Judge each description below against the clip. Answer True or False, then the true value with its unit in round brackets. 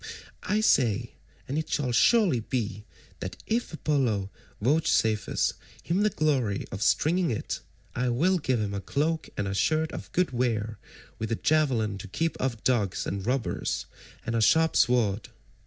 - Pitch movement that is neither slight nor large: False (6.6 semitones)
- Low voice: True (125 Hz)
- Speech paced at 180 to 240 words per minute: False (150 wpm)